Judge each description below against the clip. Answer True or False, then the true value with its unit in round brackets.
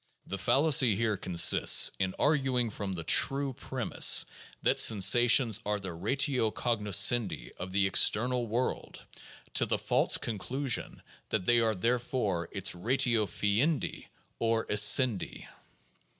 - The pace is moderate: False (125 wpm)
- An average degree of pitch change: True (4.0 semitones)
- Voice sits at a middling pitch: False (115 Hz)